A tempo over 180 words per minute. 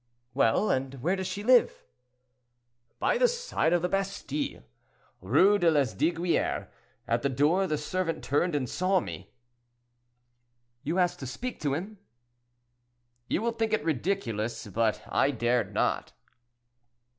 No: slow, 135 wpm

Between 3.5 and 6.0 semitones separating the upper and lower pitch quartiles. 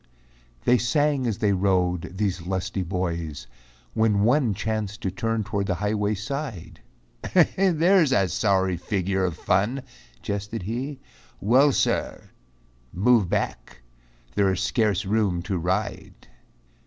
Yes: average, 3.8 semitones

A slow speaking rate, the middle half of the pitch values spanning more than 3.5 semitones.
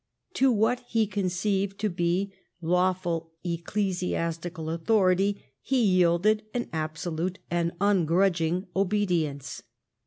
No: slow, 95 wpm; average, 3.0 semitones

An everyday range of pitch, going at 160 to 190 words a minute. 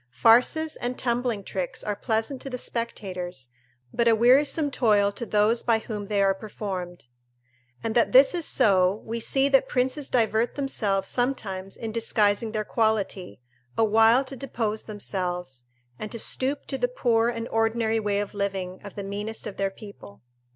Yes: average, 3.3 semitones; average, 165 wpm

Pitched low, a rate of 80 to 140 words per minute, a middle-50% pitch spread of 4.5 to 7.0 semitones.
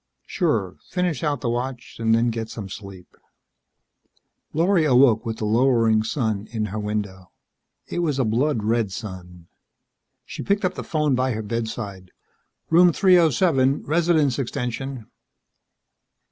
Yes: low, 120 Hz; slow, 135 wpm; wide, 5.6 semitones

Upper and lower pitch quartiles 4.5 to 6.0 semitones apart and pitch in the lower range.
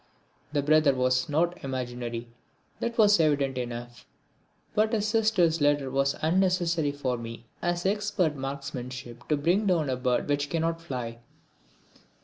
No: average, 5.3 semitones; medium, 145 Hz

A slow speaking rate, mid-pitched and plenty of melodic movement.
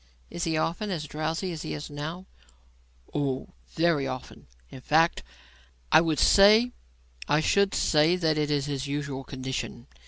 No: slow, 130 wpm; medium, 150 Hz; average, 2.8 semitones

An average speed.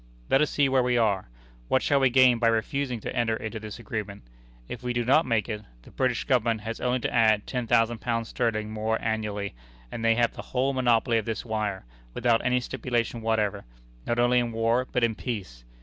No: fast, 210 wpm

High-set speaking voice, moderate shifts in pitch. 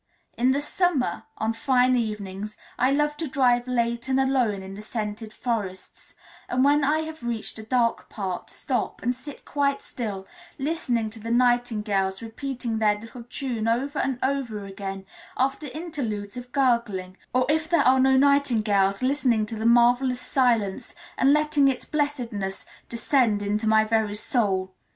Yes: high, 240 Hz; average, 3.9 semitones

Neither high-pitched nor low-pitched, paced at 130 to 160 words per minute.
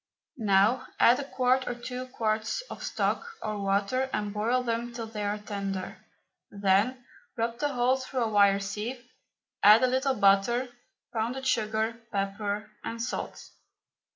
No: high, 225 Hz; average, 150 wpm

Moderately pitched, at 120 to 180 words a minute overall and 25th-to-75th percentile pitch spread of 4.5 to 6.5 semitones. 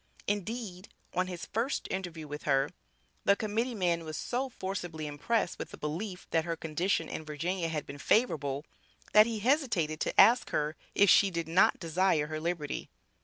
Yes: medium, 175 Hz; average, 170 wpm; average, 4.9 semitones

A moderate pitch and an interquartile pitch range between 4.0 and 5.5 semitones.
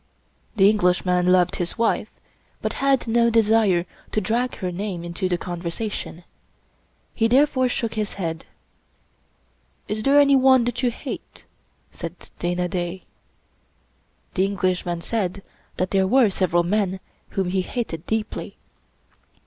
No: high, 195 Hz; average, 4.4 semitones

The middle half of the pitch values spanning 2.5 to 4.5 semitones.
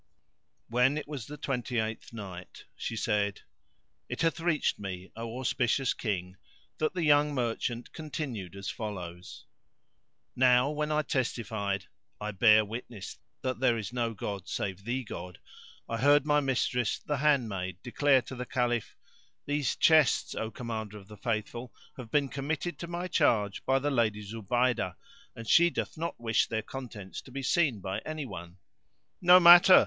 No: wide, 5.4 semitones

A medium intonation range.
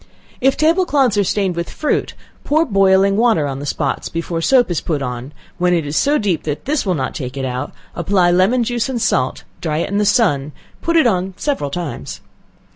No: wide, 8.2 semitones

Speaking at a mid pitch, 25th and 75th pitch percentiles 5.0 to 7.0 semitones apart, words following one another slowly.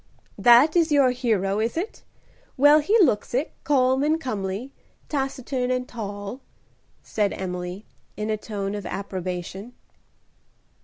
No: high, 235 Hz; average, 5.3 semitones; slow, 125 wpm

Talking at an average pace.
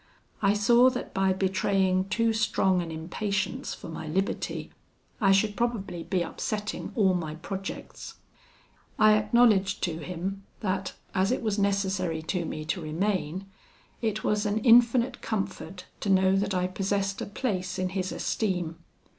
Yes: average, 150 wpm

